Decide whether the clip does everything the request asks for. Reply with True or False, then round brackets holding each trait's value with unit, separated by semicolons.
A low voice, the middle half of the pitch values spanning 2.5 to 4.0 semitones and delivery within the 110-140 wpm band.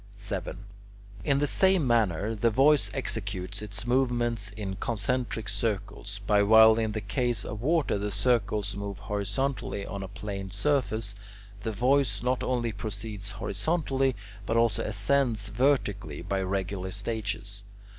True (110 Hz; 3.4 semitones; 135 wpm)